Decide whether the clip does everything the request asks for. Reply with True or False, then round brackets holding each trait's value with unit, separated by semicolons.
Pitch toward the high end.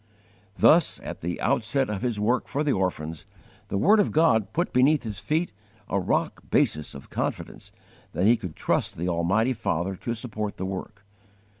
False (110 Hz)